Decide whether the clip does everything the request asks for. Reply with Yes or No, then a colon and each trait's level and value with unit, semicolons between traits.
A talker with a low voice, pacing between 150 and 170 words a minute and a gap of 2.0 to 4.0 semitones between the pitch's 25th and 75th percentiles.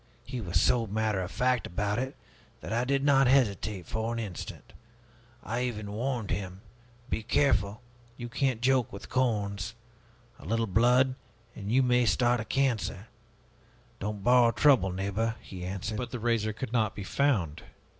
Yes: low, 115 Hz; average, 165 wpm; average, 3.6 semitones